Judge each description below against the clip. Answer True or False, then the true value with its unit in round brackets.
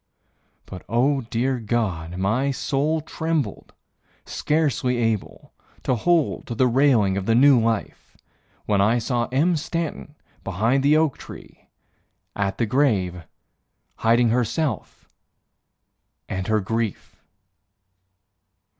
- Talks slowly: True (110 wpm)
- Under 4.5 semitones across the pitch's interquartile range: False (4.8 semitones)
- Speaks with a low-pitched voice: True (120 Hz)